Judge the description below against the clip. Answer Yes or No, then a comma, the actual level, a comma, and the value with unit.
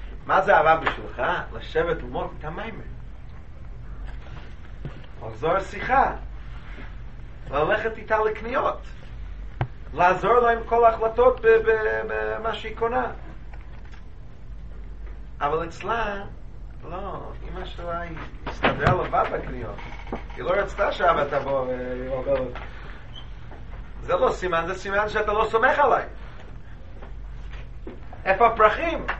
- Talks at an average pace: No, slow, 95 wpm